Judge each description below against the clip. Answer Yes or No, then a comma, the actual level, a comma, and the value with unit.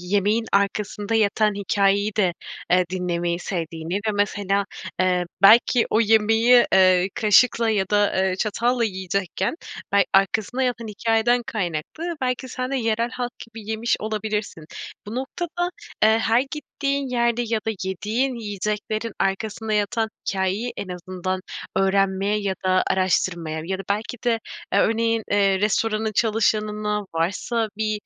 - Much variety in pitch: No, average, 3.0 semitones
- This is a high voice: Yes, high, 210 Hz